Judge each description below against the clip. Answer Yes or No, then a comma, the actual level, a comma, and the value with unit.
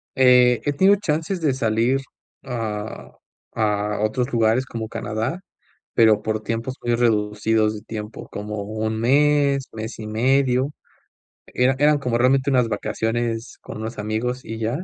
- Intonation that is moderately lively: Yes, average, 3.1 semitones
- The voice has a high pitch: No, low, 115 Hz